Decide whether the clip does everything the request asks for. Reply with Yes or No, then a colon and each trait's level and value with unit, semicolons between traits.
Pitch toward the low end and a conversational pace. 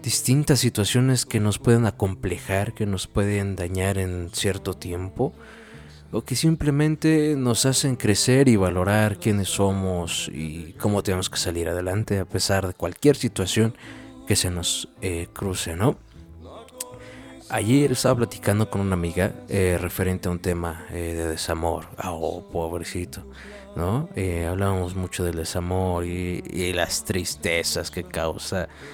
Yes: very low, 95 Hz; average, 140 wpm